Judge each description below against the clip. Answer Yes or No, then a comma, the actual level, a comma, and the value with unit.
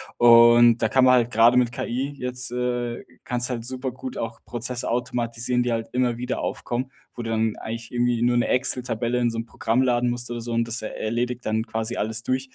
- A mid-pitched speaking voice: No, low, 120 Hz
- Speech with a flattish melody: Yes, narrow, 1.2 semitones